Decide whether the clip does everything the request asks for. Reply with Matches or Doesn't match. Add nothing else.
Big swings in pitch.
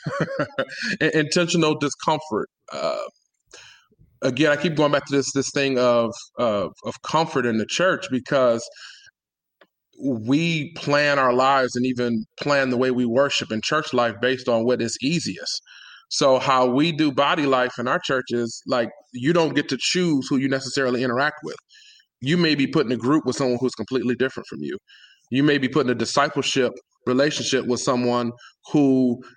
Doesn't match